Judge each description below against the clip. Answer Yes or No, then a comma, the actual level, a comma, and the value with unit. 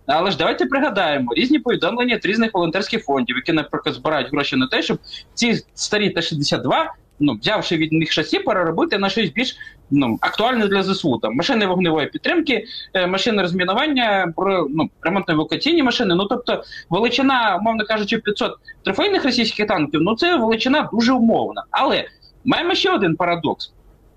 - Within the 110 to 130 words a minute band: No, fast, 155 wpm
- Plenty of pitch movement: Yes, wide, 6.9 semitones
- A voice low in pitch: No, high, 210 Hz